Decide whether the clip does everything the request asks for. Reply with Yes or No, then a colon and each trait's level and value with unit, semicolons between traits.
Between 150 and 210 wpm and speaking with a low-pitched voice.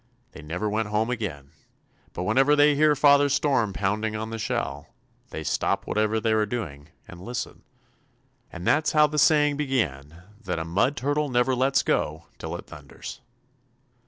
Yes: average, 165 wpm; low, 110 Hz